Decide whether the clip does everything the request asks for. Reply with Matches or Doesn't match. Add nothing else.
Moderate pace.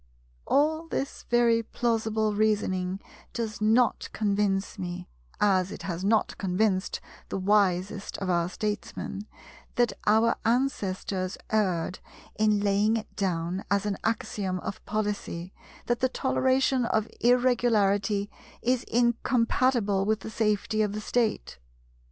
Doesn't match